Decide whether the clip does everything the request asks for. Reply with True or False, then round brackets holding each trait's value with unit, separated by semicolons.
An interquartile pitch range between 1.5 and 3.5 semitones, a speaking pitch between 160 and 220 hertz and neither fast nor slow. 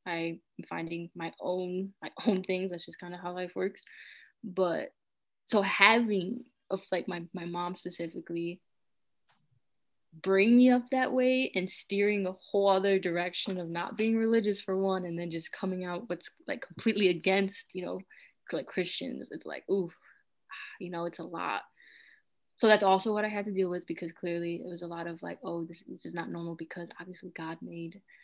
True (3.1 semitones; 185 Hz; 185 wpm)